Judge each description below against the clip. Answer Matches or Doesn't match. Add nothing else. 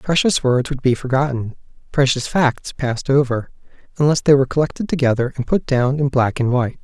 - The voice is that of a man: Matches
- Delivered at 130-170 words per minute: Doesn't match